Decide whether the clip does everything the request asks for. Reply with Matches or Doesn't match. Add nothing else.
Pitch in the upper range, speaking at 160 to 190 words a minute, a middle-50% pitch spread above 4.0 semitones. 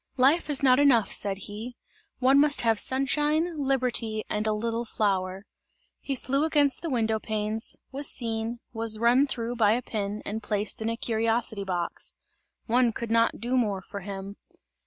Doesn't match